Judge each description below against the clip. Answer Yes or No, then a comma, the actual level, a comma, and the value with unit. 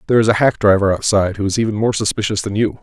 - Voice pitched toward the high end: No, low, 105 Hz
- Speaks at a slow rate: No, fast, 275 wpm